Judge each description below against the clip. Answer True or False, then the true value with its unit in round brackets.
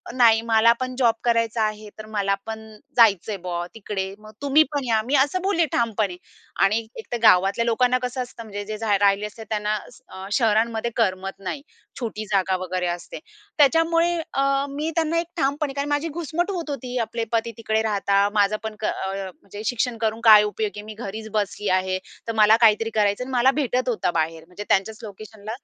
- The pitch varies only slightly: False (3.7 semitones)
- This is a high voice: True (220 Hz)